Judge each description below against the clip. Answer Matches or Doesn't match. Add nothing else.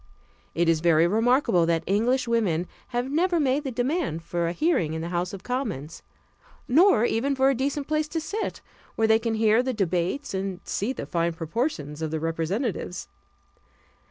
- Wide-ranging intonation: Matches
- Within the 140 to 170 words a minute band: Doesn't match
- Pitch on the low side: Doesn't match